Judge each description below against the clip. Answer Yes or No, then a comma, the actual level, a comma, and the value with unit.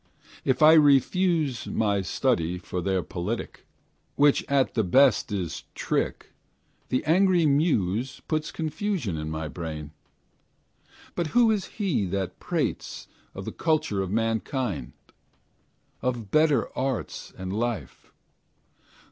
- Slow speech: Yes, slow, 120 wpm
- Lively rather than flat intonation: Yes, wide, 8.5 semitones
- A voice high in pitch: No, low, 125 Hz